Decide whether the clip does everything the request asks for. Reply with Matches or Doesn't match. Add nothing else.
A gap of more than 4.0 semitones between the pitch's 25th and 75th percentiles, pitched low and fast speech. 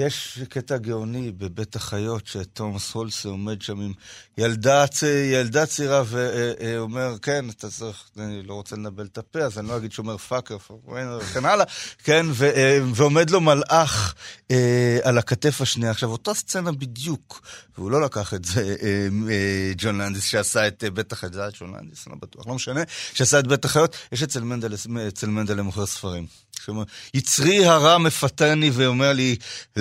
Matches